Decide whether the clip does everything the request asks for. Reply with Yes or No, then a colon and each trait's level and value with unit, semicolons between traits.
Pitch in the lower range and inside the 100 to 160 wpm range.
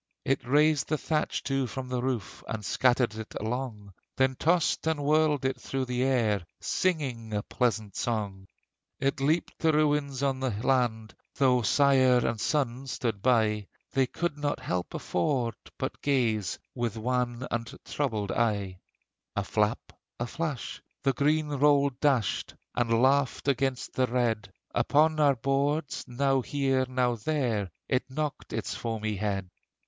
Yes: low, 130 Hz; average, 150 wpm